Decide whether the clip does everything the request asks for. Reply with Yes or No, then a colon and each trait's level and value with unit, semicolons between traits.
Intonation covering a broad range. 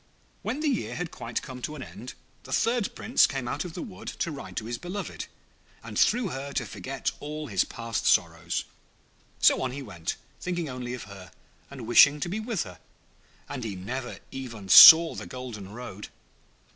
Yes: wide, 6.3 semitones